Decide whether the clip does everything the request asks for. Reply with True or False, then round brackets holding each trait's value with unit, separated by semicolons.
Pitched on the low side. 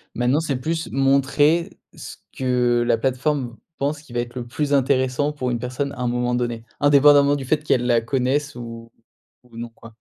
True (130 Hz)